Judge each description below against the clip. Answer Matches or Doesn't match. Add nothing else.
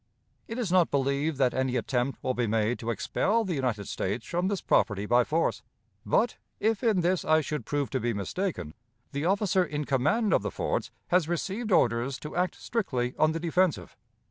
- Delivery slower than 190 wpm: Doesn't match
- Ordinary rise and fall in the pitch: Doesn't match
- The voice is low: Doesn't match